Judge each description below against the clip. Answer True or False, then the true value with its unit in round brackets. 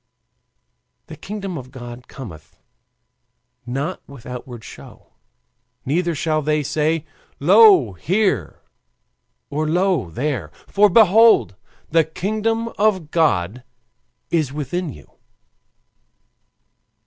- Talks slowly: True (95 wpm)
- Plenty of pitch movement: True (6.7 semitones)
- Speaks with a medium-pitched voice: True (155 Hz)